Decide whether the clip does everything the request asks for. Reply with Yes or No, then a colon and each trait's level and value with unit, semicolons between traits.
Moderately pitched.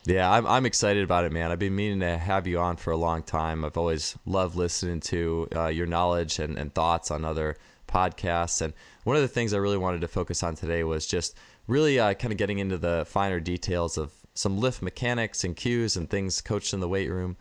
No: very low, 90 Hz